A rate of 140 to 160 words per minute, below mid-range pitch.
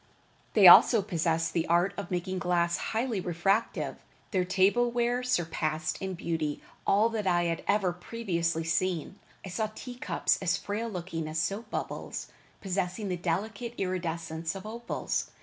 No: average, 150 wpm; medium, 185 Hz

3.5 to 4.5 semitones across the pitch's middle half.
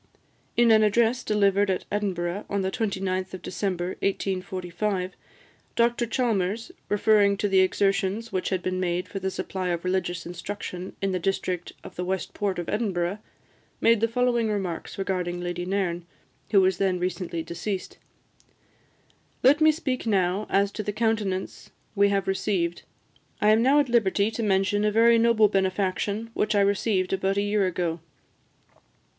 No: narrow, 2.5 semitones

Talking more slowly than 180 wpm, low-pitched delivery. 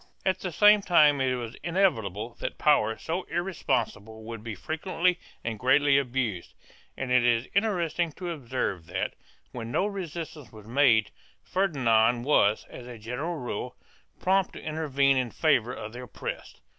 Yes: average, 155 wpm; low, 130 Hz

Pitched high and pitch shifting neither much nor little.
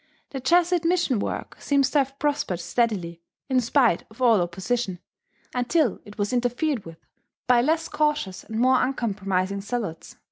No: high, 245 Hz; wide, 5.9 semitones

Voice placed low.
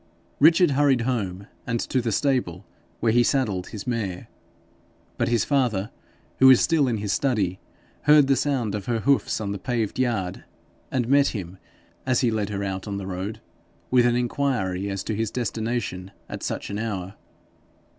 Yes: low, 115 Hz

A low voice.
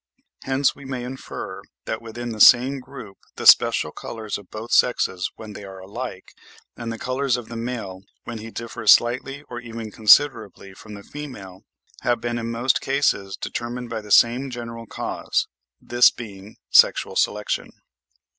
Yes: low, 115 Hz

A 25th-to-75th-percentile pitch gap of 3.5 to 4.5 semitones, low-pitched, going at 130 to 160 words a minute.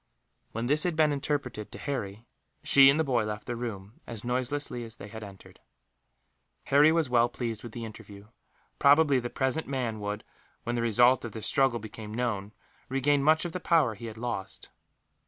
No: average, 4.2 semitones; low, 120 Hz; average, 190 wpm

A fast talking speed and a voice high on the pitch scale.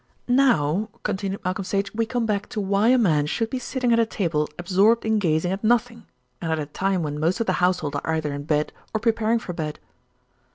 Yes: fast, 220 wpm; high, 195 Hz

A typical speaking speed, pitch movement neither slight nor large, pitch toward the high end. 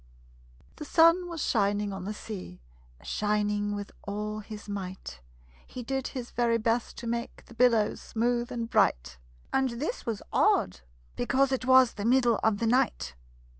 Yes: average, 160 wpm; average, 3.3 semitones; high, 230 Hz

